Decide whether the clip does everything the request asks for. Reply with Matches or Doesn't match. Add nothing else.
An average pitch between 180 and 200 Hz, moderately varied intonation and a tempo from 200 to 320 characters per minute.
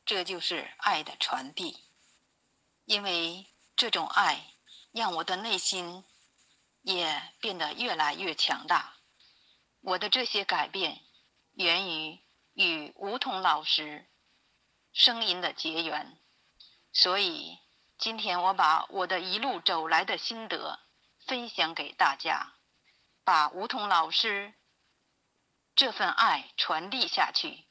Doesn't match